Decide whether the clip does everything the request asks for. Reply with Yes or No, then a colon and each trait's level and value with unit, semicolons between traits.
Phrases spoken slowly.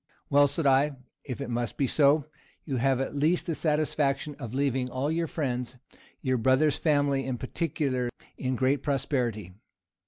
No: average, 160 wpm